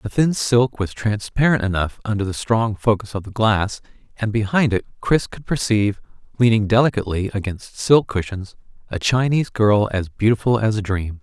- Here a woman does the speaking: No, male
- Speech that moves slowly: No, average, 170 wpm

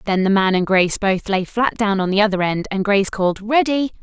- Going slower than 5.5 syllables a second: No, 5.9 syllables/s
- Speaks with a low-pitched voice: No, high, 200 Hz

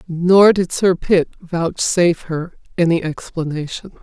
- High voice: No, medium, 170 Hz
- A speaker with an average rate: No, slow, 120 wpm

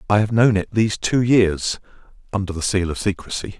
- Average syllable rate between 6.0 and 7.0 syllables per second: No, 5.6 syllables/s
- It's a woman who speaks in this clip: No, male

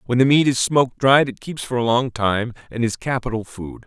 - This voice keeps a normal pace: No, fast, 250 wpm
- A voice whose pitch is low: Yes, low, 120 Hz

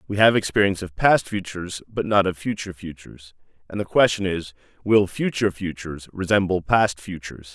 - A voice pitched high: No, very low, 95 Hz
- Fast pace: No, average, 165 wpm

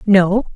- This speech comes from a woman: Yes, female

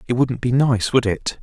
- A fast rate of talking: Yes, fast, 250 wpm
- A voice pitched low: Yes, low, 125 Hz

